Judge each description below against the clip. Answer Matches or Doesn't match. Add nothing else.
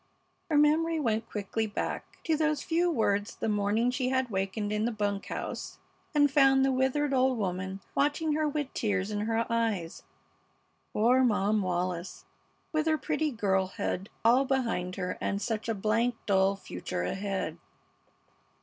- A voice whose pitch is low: Doesn't match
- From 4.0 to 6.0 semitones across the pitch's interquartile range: Matches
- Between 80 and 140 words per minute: Doesn't match